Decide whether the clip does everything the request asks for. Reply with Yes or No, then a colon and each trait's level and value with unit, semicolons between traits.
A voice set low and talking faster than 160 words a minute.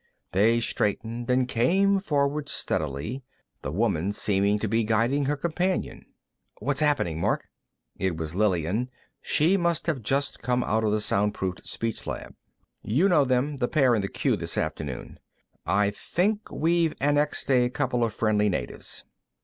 No: low, 120 Hz; average, 155 wpm